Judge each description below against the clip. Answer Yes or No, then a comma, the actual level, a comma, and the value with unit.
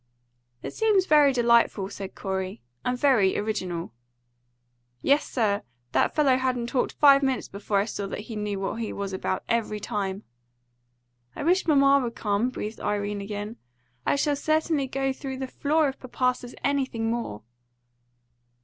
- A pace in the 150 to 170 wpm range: Yes, average, 160 wpm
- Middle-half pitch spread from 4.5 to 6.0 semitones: Yes, average, 5.2 semitones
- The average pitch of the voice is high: Yes, high, 235 Hz